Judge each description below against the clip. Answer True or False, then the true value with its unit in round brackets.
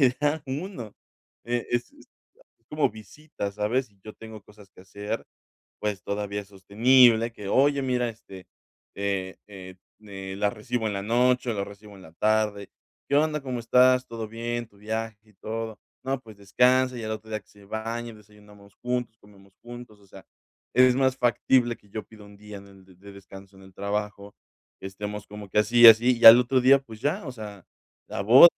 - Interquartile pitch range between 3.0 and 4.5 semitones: True (3.3 semitones)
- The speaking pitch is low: True (110 Hz)